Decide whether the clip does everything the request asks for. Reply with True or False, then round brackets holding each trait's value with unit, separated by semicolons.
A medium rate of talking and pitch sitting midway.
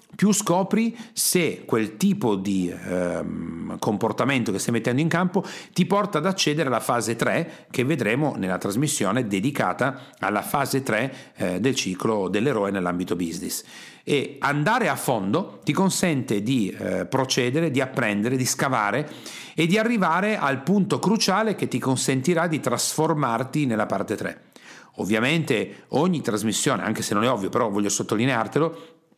True (150 wpm; 150 Hz)